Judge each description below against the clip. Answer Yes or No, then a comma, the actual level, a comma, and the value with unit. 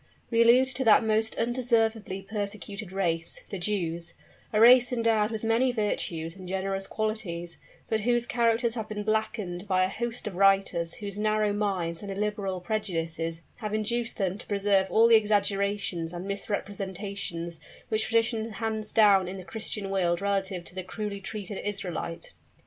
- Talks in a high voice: Yes, high, 205 Hz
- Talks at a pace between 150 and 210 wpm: Yes, average, 160 wpm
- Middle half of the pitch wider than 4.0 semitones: No, average, 2.7 semitones